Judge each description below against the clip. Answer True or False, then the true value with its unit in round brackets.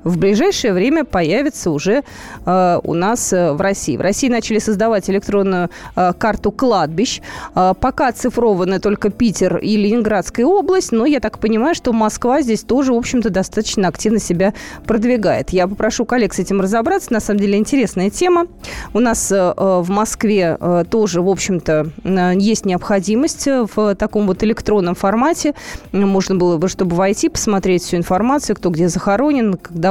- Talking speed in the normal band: False (165 wpm)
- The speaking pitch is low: False (205 Hz)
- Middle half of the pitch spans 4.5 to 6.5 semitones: False (4.1 semitones)